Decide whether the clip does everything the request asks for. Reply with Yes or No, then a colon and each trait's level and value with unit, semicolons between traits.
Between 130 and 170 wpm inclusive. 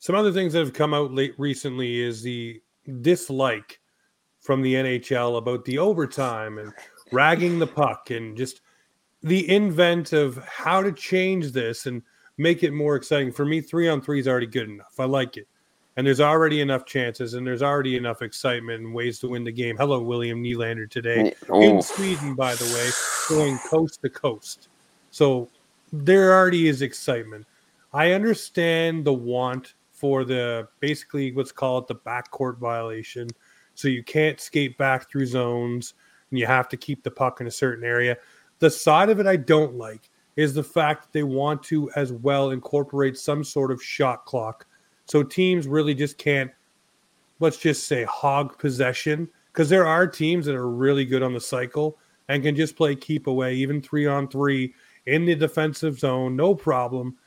No: average, 180 wpm